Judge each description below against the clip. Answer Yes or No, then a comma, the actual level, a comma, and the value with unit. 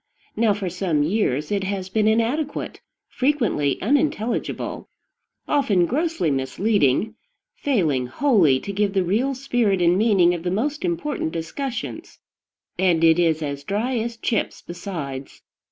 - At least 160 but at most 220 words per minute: No, slow, 135 wpm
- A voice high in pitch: Yes, high, 200 Hz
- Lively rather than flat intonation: Yes, wide, 6.2 semitones